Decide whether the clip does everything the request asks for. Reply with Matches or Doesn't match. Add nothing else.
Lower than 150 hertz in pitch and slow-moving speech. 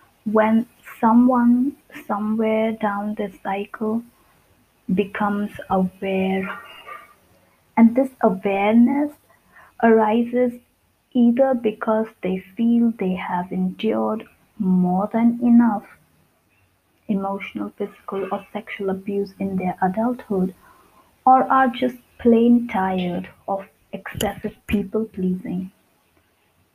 Doesn't match